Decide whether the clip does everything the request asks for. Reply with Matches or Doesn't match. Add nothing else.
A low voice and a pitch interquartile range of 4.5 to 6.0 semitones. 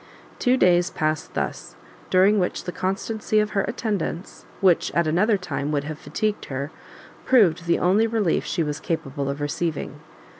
Doesn't match